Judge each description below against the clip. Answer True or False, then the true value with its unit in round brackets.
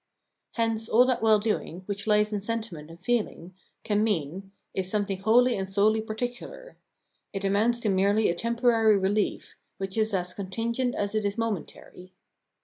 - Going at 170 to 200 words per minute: False (160 wpm)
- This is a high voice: True (210 Hz)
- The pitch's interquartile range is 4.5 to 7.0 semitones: False (2.8 semitones)